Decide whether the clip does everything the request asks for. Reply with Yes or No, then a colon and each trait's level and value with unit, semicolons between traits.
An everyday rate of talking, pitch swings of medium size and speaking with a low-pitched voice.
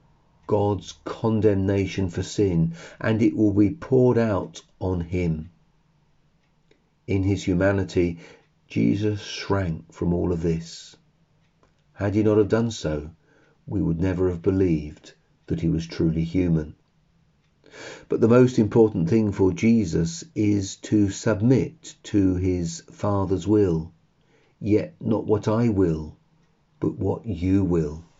No: slow, 130 wpm; average, 4.3 semitones; low, 100 Hz